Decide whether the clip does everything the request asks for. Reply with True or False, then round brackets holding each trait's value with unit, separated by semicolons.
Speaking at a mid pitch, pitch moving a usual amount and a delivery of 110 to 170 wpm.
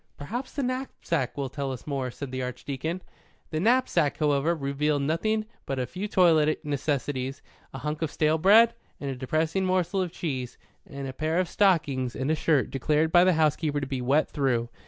False (150 Hz; 4.1 semitones; 190 wpm)